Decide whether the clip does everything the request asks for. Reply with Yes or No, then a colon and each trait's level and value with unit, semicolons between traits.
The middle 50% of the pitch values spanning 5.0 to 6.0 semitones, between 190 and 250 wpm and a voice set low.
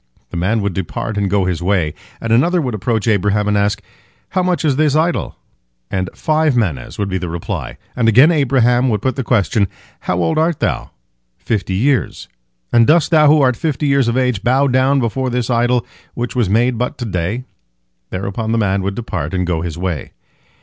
Yes: wide, 5.6 semitones; average, 195 wpm; low, 115 Hz